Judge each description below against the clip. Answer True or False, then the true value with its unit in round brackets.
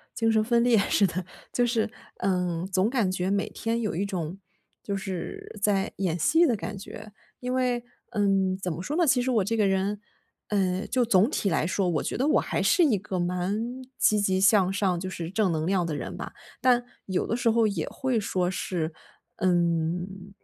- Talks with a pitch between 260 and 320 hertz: False (195 Hz)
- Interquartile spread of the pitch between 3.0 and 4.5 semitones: True (3.8 semitones)